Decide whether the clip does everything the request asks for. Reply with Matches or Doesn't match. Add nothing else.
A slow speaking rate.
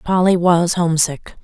Matches